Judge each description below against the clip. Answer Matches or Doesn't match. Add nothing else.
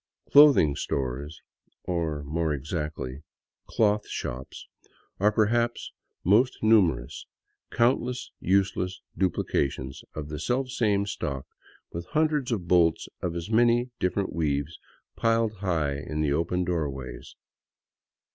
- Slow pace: Matches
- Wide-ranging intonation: Matches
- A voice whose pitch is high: Doesn't match